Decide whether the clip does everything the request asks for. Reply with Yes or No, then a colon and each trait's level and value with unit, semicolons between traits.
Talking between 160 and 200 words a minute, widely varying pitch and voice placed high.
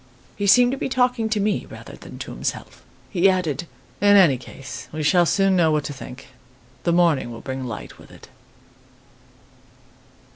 No: average, 175 wpm; wide, 6.1 semitones; medium, 175 Hz